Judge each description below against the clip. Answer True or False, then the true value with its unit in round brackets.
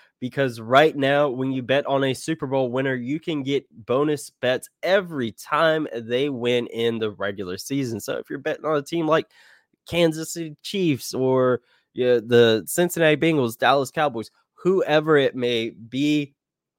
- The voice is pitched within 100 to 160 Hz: True (135 Hz)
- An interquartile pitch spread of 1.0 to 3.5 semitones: False (4.1 semitones)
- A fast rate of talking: False (170 wpm)